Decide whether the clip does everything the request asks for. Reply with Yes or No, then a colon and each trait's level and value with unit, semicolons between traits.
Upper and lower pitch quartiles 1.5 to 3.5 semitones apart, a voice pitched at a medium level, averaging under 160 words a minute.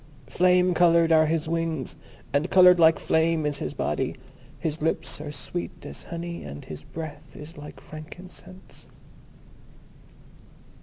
Yes: narrow, 2.5 semitones; medium, 160 Hz; slow, 135 wpm